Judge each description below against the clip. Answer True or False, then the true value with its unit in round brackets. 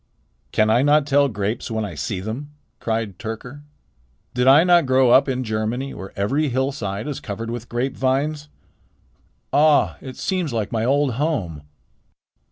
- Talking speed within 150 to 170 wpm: True (155 wpm)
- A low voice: True (125 Hz)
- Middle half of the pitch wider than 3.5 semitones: True (4.6 semitones)